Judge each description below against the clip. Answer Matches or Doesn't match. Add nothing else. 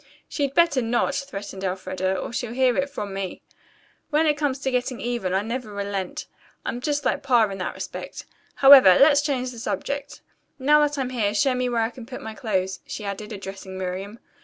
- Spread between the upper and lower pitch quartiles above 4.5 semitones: Matches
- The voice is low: Doesn't match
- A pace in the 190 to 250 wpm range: Matches